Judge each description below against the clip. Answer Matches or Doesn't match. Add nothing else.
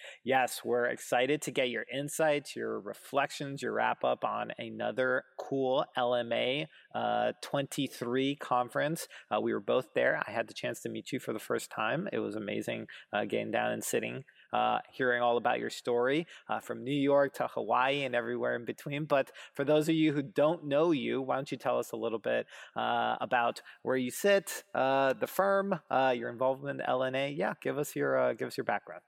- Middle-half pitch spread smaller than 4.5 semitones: Matches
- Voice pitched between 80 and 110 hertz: Doesn't match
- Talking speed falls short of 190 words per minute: Doesn't match